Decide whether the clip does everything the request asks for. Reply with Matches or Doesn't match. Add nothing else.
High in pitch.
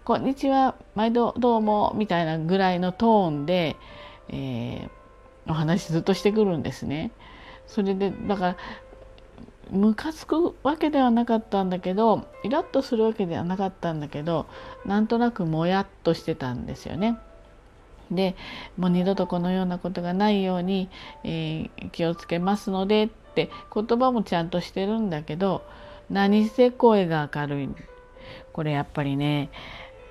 Matches